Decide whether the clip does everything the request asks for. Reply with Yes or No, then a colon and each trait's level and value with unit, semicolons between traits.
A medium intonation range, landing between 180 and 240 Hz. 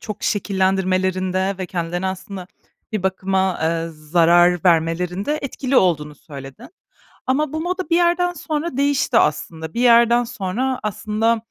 No: wide, 5.9 semitones; high, 190 Hz